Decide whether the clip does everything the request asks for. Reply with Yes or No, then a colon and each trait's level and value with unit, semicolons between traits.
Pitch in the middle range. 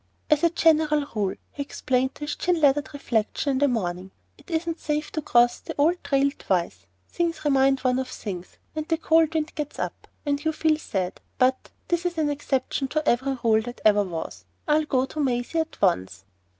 No: very high, 280 Hz